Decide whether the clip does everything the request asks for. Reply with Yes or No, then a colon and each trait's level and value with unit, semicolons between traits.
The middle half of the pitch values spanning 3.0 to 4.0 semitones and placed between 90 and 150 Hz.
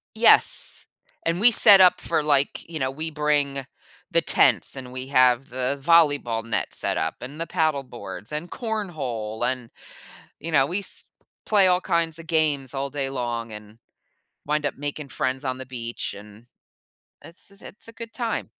No: average, 4.7 semitones; medium, 140 Hz